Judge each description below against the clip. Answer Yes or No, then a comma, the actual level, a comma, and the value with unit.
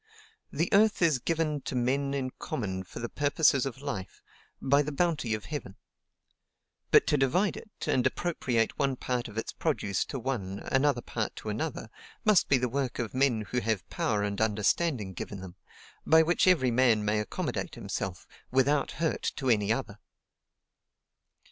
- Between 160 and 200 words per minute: Yes, average, 165 wpm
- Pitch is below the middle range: Yes, low, 130 Hz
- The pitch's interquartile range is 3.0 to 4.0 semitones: No, average, 5.1 semitones